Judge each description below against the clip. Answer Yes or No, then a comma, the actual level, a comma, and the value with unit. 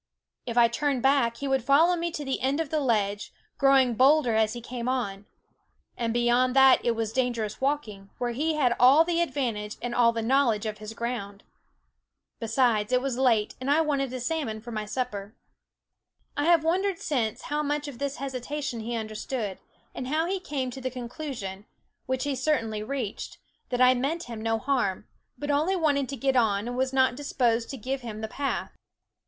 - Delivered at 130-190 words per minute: No, average, 200 wpm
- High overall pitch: Yes, very high, 255 Hz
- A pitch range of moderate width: Yes, average, 3.7 semitones